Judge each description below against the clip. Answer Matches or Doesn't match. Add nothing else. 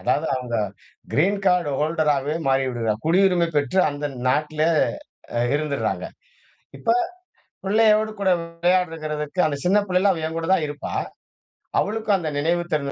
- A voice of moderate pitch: Matches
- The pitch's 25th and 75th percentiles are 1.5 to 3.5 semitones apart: Doesn't match